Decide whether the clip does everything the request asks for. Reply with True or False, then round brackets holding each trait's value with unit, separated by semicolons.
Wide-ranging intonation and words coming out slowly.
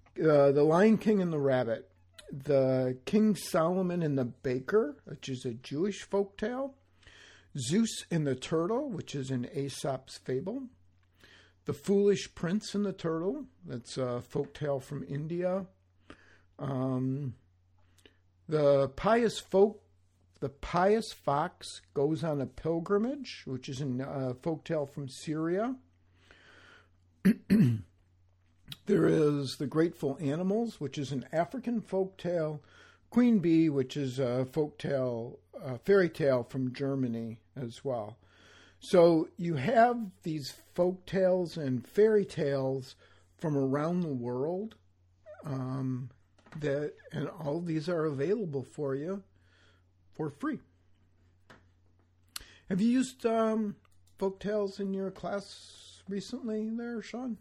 True (7.6 semitones; 120 wpm)